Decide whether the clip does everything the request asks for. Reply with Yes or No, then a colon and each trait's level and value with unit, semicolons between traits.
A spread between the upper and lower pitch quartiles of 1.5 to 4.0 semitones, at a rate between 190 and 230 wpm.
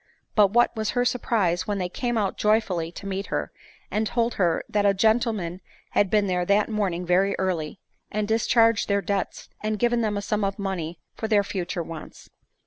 Yes: average, 3.0 semitones; average, 195 wpm